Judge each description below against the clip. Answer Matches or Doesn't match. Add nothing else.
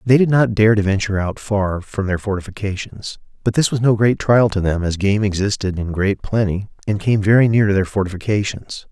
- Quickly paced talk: Matches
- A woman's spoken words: Doesn't match